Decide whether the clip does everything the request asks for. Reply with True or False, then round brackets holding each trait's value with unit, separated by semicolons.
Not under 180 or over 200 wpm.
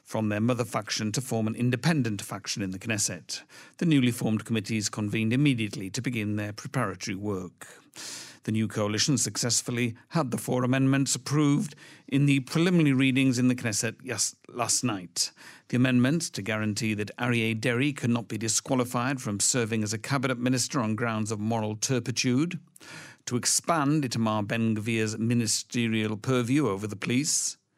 False (160 wpm)